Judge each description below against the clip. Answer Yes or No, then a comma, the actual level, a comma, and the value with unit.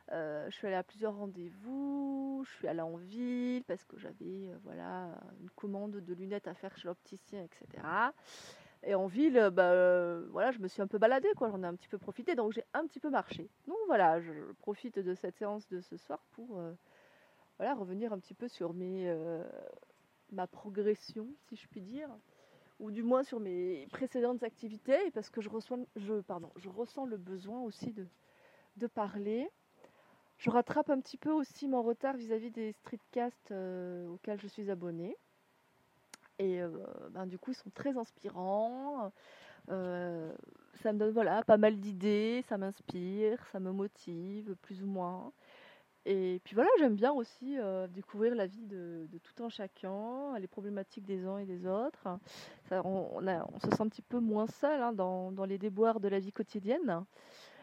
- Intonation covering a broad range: No, average, 4.4 semitones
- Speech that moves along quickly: No, average, 190 wpm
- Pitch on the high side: Yes, high, 210 Hz